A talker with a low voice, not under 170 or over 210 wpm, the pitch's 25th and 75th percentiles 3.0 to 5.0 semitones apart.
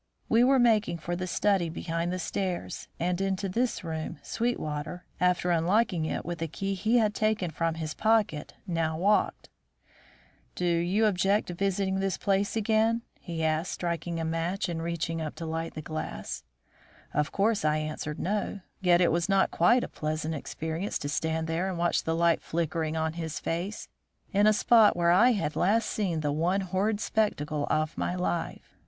No: medium, 175 Hz; average, 180 wpm; average, 3.6 semitones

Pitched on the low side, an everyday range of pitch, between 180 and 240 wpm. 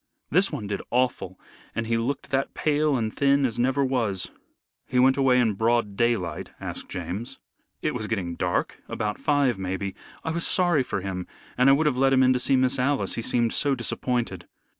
Yes: low, 125 Hz; average, 4.2 semitones; average, 200 wpm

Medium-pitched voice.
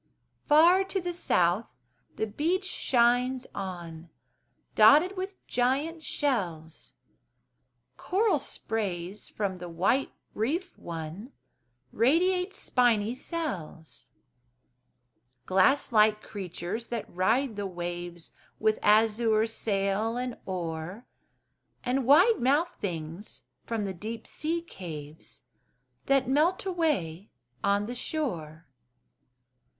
No: high, 225 Hz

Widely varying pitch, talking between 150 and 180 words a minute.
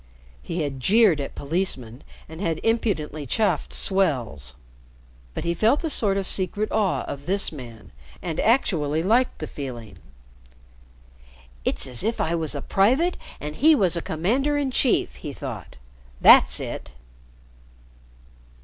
No: wide, 7.3 semitones; average, 140 wpm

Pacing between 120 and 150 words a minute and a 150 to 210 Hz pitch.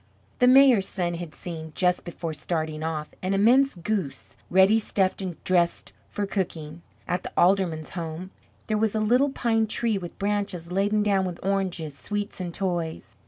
No: average, 165 wpm; medium, 185 Hz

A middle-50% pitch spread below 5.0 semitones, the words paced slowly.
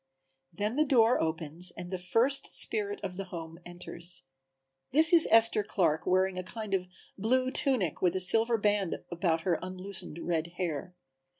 No: average, 4.6 semitones; average, 165 wpm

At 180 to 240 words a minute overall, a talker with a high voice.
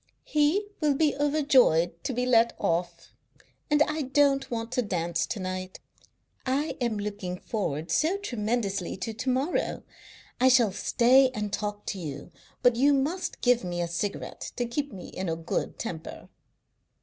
No: average, 160 wpm; high, 235 Hz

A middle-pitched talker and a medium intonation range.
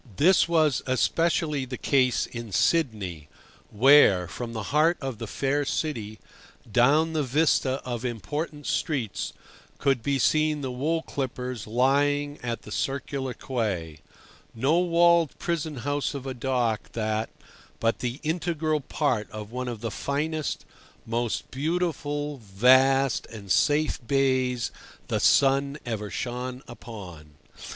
No: low, 130 Hz; average, 4.1 semitones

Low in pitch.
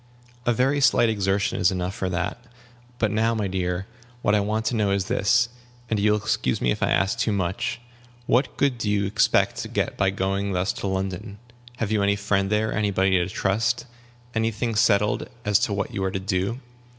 Yes: low, 100 Hz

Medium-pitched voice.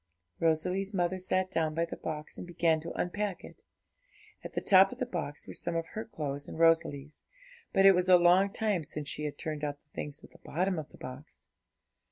Yes: medium, 170 Hz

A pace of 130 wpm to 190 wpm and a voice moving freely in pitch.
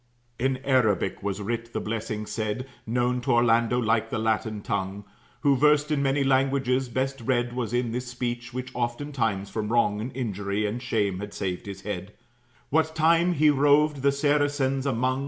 No: average, 175 wpm; average, 3.8 semitones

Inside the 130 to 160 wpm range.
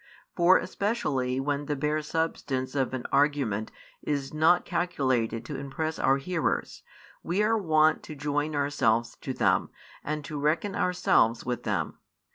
Yes: average, 145 wpm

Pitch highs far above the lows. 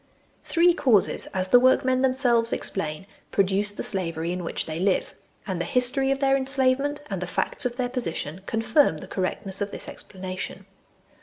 Yes: wide, 5.8 semitones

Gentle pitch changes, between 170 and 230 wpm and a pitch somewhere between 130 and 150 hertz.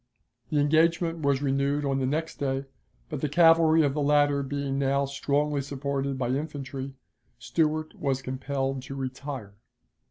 No: narrow, 1.7 semitones; average, 150 wpm; medium, 140 Hz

